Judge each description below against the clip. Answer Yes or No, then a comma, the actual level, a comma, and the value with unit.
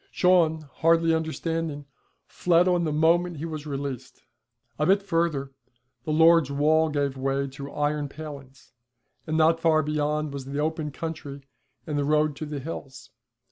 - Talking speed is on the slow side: No, average, 155 wpm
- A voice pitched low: No, medium, 155 Hz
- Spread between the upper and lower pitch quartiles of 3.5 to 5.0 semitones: No, narrow, 2.5 semitones